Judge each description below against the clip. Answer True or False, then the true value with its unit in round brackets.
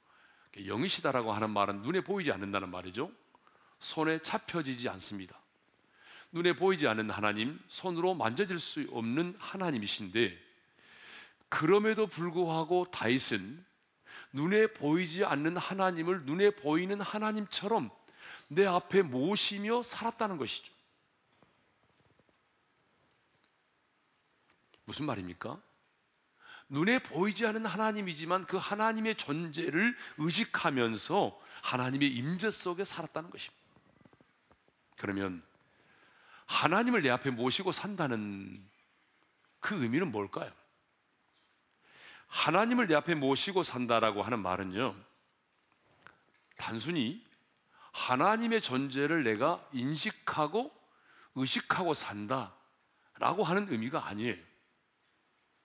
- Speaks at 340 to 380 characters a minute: False (245 characters per minute)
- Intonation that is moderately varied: False (7.9 semitones)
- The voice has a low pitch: False (165 Hz)